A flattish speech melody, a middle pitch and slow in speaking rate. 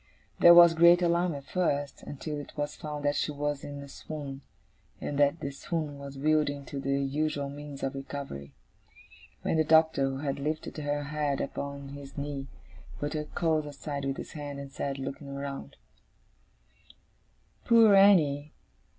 No: narrow, 1.7 semitones; medium, 145 Hz; average, 165 wpm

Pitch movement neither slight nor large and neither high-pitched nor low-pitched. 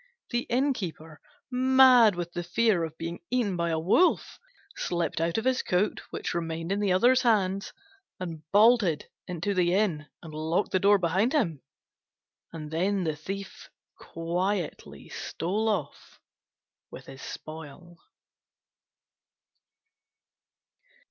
Yes: average, 4.4 semitones; medium, 180 Hz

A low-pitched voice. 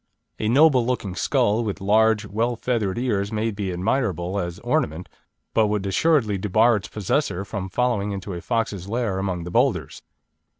Yes: low, 105 Hz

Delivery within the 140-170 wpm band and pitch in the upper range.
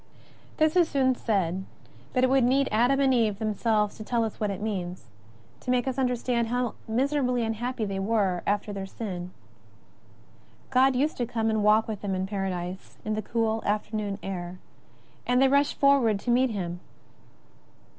No: average, 180 wpm; high, 225 Hz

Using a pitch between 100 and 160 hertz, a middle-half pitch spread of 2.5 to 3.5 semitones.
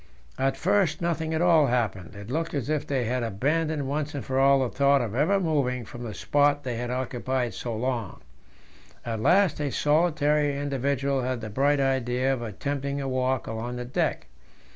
Yes: low, 135 Hz; average, 3.1 semitones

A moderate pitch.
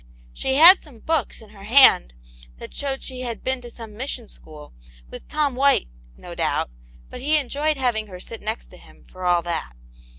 No: high, 245 Hz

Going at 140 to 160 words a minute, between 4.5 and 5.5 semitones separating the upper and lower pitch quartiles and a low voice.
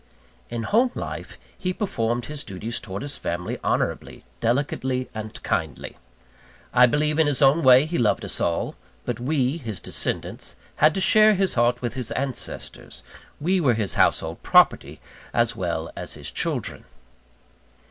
Yes: average, 155 wpm; average, 4.9 semitones; low, 125 Hz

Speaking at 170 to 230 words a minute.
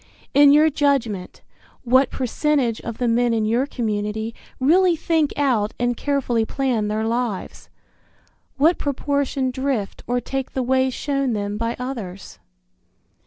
No: slow, 135 wpm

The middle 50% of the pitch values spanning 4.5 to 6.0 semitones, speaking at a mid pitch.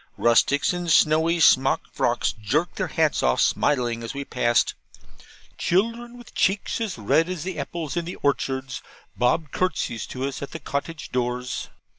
Yes: wide, 5.6 semitones; medium, 145 Hz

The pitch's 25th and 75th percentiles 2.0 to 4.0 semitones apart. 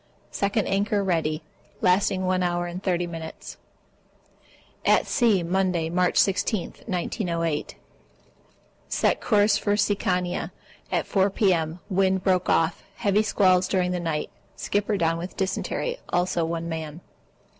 Yes: average, 2.7 semitones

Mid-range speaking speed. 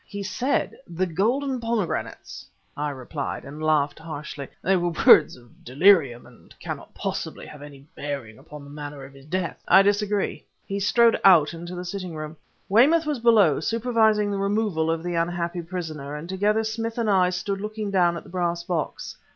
Yes: average, 180 wpm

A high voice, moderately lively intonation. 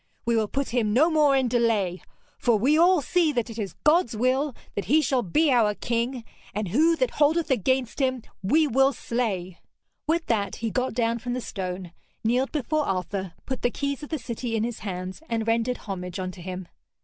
Yes: high, 240 Hz; average, 4.8 semitones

